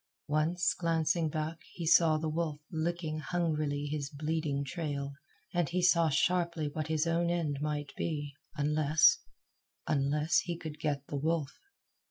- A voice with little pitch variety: Yes, narrow, 2.3 semitones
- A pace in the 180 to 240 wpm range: No, average, 145 wpm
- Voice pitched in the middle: Yes, medium, 155 Hz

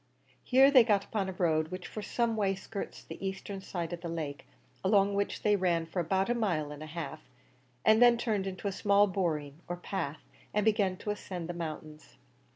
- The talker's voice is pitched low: No, high, 190 Hz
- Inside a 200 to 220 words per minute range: Yes, fast, 205 wpm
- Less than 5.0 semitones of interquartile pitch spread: Yes, average, 3.8 semitones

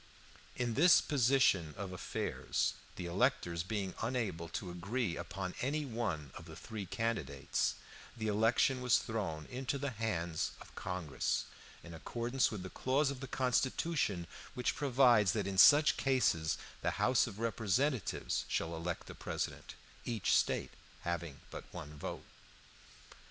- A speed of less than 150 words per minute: Yes, average, 140 wpm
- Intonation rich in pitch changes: Yes, wide, 6.4 semitones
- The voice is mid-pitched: No, low, 110 Hz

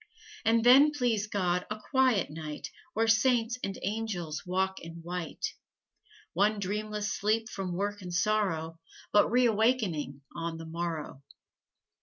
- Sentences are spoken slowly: Yes, slow, 130 wpm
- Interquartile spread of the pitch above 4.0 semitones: Yes, average, 4.7 semitones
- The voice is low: No, high, 205 Hz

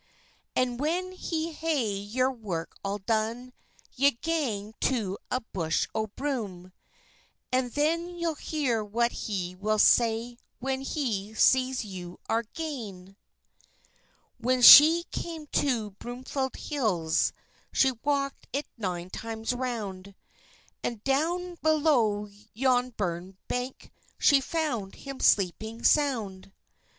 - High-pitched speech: Yes, high, 240 Hz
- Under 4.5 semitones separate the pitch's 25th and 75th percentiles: No, wide, 5.4 semitones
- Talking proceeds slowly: Yes, slow, 115 wpm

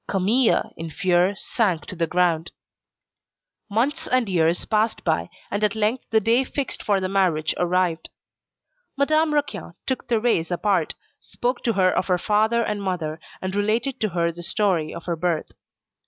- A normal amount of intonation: Yes, average, 4.5 semitones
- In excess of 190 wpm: No, average, 165 wpm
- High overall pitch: Yes, high, 195 Hz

